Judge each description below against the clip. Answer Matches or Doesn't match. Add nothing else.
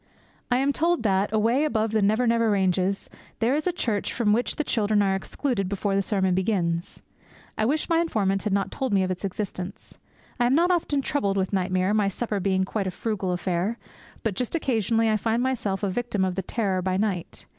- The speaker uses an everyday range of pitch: Matches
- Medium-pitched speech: Doesn't match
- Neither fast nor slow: Doesn't match